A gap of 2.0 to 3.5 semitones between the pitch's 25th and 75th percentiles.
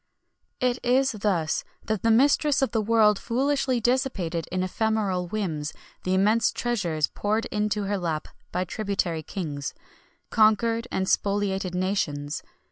No: average, 4.1 semitones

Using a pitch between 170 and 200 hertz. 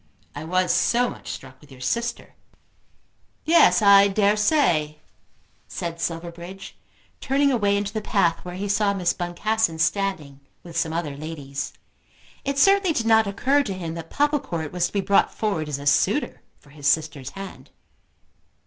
Yes: medium, 185 Hz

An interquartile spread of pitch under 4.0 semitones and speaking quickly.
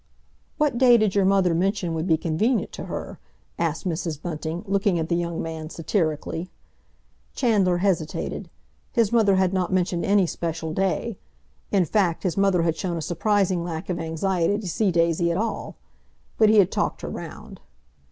No: average, 3.2 semitones; average, 170 wpm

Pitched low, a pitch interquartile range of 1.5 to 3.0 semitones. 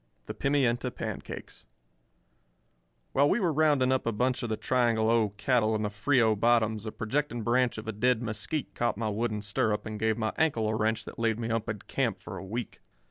Yes: low, 115 Hz; narrow, 2.6 semitones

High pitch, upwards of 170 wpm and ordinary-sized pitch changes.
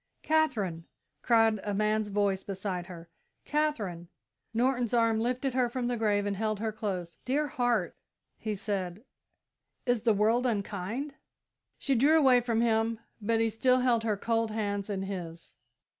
No: high, 220 Hz; average, 155 wpm; average, 3.4 semitones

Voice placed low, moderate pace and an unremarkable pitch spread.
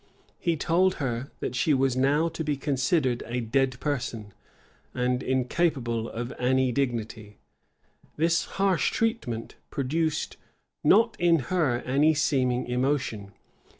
No: low, 130 Hz; slow, 125 wpm; average, 4.3 semitones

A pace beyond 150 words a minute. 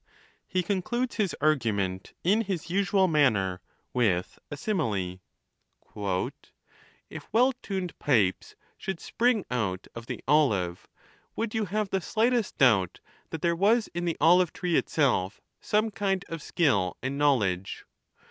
No: average, 140 wpm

